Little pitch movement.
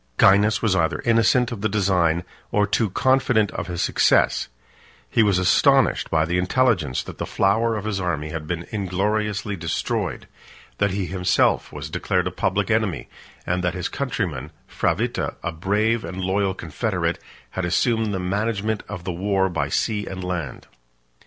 No: average, 3.3 semitones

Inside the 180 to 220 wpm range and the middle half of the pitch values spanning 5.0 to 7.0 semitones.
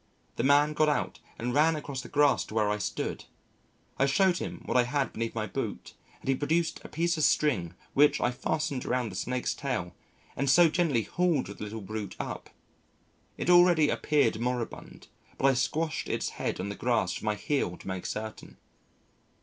Yes: average, 190 wpm; wide, 5.5 semitones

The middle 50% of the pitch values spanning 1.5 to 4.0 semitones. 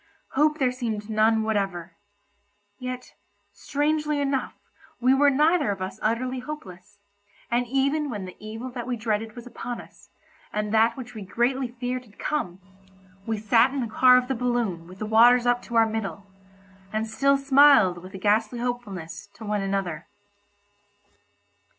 Yes: average, 3.7 semitones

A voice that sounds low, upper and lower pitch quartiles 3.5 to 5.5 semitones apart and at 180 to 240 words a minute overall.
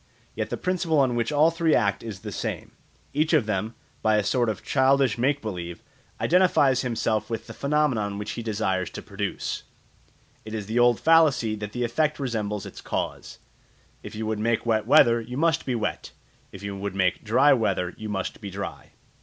Yes: low, 115 Hz; average, 4.8 semitones; average, 195 wpm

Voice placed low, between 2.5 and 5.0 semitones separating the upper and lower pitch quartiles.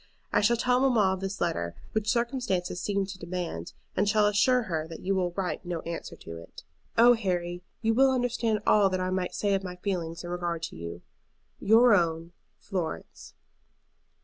No: high, 190 Hz; average, 4.1 semitones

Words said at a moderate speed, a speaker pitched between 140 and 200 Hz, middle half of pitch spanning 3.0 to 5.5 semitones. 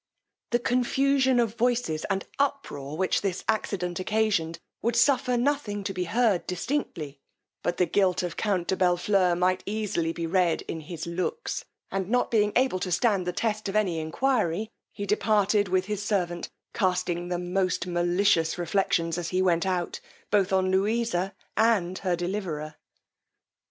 Yes: average, 150 wpm; high, 190 Hz; average, 3.8 semitones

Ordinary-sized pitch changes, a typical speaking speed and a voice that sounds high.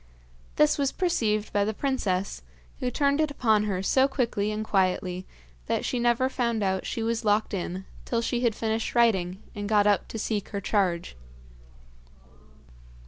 Yes: average, 3.3 semitones; average, 165 wpm; high, 215 Hz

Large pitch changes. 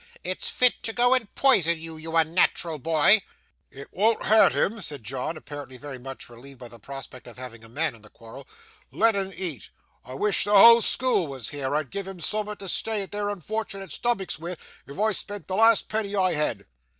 Yes: wide, 7.3 semitones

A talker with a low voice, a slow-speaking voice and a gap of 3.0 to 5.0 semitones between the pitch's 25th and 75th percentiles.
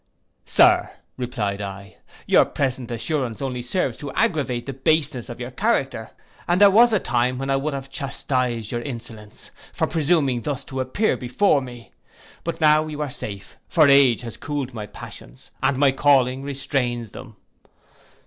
No: low, 130 Hz; average, 165 wpm; average, 3.3 semitones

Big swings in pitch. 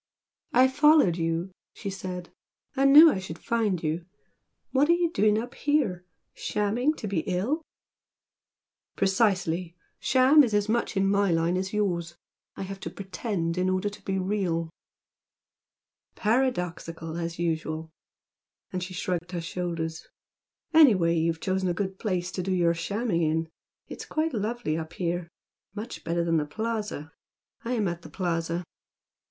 No: average, 4.3 semitones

